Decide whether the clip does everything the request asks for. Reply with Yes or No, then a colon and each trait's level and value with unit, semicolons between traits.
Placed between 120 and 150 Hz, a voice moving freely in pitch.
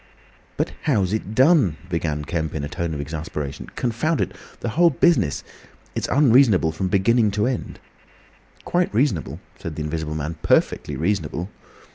No: very low, 95 Hz; wide, 7.5 semitones